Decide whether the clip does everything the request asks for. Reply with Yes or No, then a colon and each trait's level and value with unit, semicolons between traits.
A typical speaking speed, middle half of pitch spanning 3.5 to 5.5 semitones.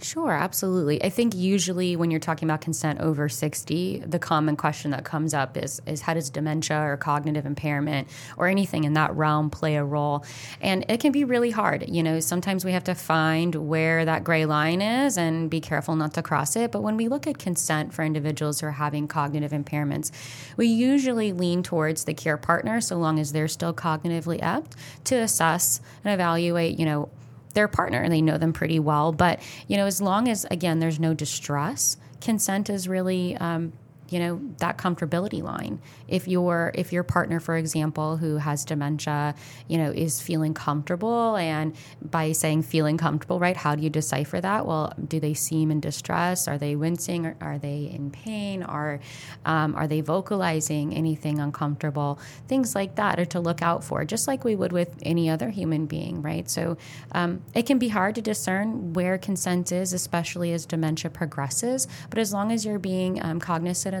No: average, 195 wpm; average, 3.1 semitones